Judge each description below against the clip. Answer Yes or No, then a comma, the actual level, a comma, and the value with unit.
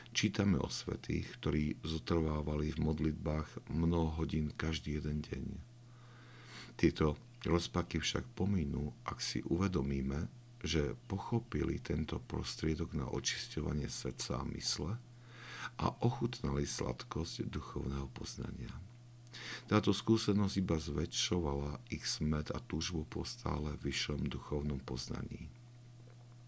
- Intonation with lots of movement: Yes, wide, 7.0 semitones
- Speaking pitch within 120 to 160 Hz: No, very low, 80 Hz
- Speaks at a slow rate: Yes, slow, 105 wpm